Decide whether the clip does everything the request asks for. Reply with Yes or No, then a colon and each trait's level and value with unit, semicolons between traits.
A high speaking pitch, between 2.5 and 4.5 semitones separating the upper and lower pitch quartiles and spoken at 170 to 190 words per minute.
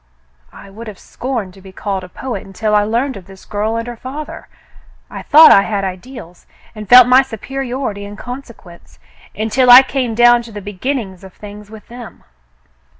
Yes: high, 220 Hz; average, 4.0 semitones; average, 185 wpm